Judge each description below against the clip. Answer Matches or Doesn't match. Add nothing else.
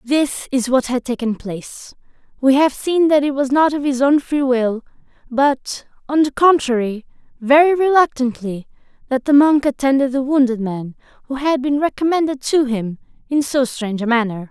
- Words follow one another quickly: Doesn't match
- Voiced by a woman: Matches